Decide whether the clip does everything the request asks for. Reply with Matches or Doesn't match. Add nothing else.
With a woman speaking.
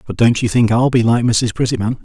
Doesn't match